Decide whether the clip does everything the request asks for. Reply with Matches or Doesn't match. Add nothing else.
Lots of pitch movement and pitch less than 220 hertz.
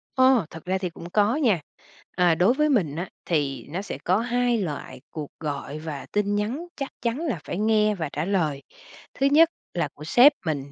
Matches